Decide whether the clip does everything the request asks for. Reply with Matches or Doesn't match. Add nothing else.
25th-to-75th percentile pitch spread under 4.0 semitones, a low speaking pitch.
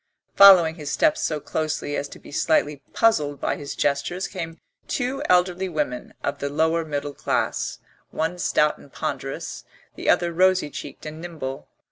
Doesn't match